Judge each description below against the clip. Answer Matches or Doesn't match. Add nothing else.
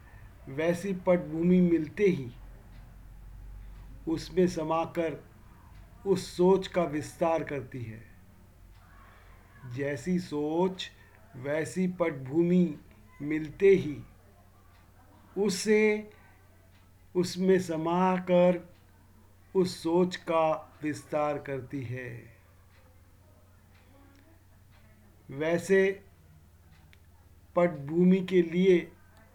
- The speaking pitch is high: Doesn't match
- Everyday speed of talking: Doesn't match